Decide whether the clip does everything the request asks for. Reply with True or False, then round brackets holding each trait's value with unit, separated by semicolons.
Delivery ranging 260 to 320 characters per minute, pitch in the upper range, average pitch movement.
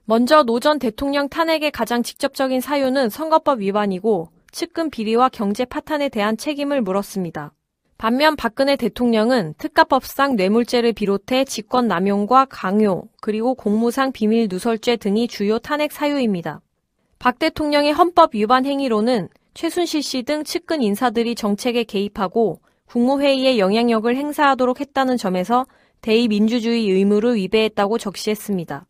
False (345 characters per minute; 240 Hz; 4.5 semitones)